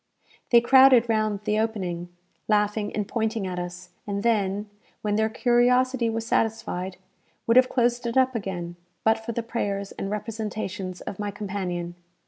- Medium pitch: No, high, 215 Hz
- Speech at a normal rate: Yes, average, 155 wpm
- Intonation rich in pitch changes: No, average, 3.0 semitones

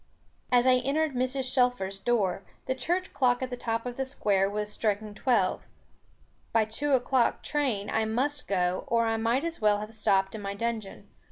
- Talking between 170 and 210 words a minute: Yes, average, 190 wpm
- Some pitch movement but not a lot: Yes, average, 3.7 semitones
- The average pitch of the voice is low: No, high, 235 Hz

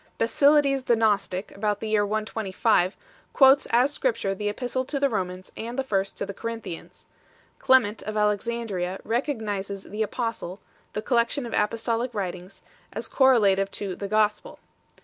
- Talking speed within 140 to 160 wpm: No, average, 170 wpm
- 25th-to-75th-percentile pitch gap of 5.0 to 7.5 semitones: No, average, 3.3 semitones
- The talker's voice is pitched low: No, high, 215 Hz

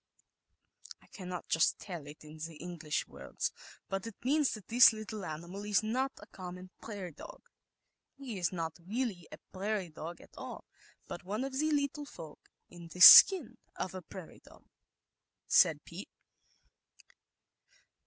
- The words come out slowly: No, average, 155 wpm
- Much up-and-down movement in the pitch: No, average, 4.8 semitones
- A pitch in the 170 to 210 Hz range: Yes, high, 190 Hz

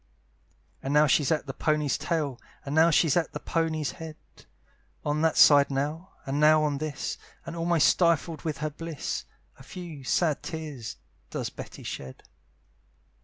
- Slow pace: No, average, 160 wpm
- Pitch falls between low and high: Yes, medium, 155 Hz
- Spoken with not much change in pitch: Yes, narrow, 2.2 semitones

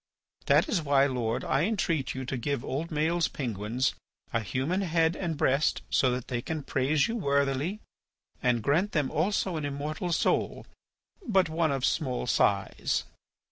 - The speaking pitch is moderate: Yes, medium, 145 Hz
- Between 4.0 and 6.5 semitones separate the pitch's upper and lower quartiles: Yes, average, 4.3 semitones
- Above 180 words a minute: No, average, 155 wpm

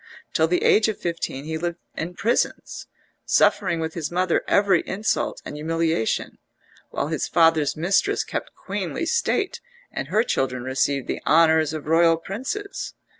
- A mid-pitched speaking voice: Yes, medium, 165 Hz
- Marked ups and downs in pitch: No, average, 3.7 semitones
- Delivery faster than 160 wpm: No, average, 150 wpm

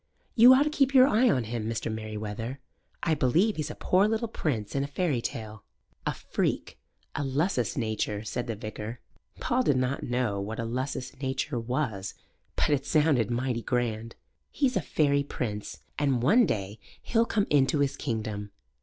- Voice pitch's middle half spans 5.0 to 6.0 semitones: Yes, wide, 5.6 semitones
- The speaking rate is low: No, average, 175 wpm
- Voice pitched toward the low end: Yes, low, 130 Hz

